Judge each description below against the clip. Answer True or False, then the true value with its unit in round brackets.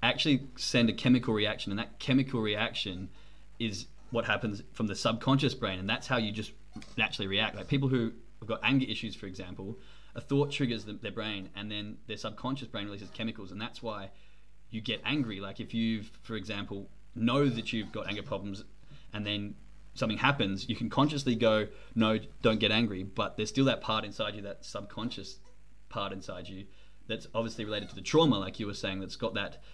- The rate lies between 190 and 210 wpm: True (200 wpm)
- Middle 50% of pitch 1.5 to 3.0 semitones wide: True (2.7 semitones)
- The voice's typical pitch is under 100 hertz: False (110 Hz)